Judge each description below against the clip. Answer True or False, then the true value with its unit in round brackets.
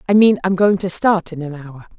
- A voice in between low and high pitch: True (180 Hz)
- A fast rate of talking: True (270 wpm)